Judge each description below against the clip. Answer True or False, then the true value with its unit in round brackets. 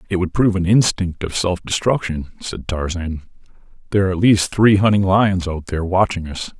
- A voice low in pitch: True (90 Hz)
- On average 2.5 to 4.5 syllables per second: False (5.6 syllables/s)